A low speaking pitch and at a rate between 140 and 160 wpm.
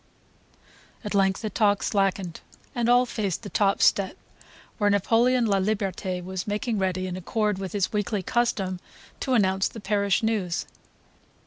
No: high, 200 Hz; average, 145 wpm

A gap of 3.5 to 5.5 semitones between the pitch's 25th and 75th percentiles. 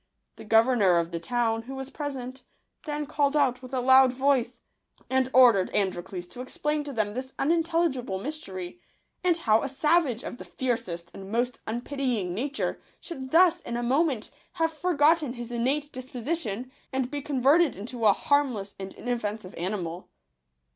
Yes: average, 4.6 semitones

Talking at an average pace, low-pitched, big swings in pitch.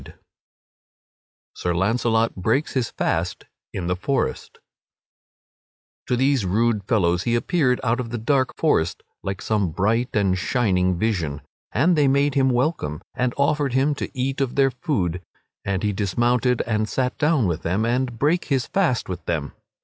Yes: average, 160 wpm; low, 120 Hz; wide, 5.7 semitones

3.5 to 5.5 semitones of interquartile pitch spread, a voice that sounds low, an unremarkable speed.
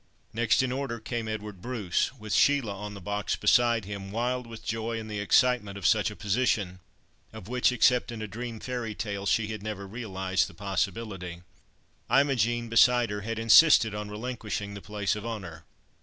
No: average, 2.8 semitones; low, 110 Hz; average, 180 wpm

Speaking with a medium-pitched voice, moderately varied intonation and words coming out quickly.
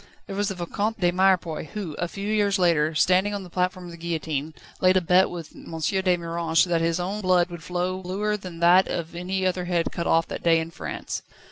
No: medium, 180 Hz; narrow, 2.0 semitones; fast, 230 wpm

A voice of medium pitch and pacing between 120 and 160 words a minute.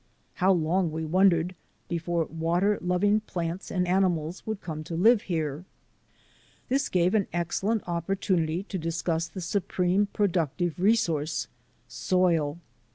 Yes: medium, 175 Hz; slow, 135 wpm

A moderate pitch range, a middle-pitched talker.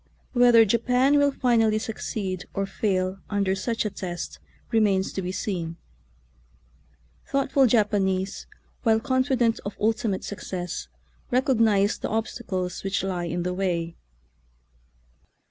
No: average, 3.6 semitones; high, 205 Hz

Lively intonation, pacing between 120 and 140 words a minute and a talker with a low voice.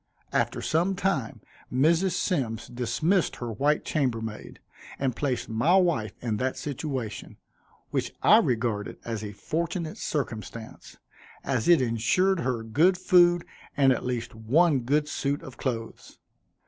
Yes: wide, 6.5 semitones; slow, 135 wpm; low, 130 Hz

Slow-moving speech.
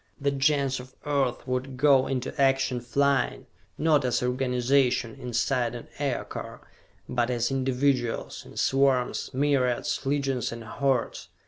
Yes: slow, 125 wpm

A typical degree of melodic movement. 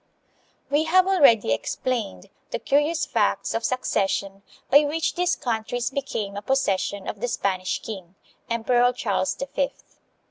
No: wide, 5.8 semitones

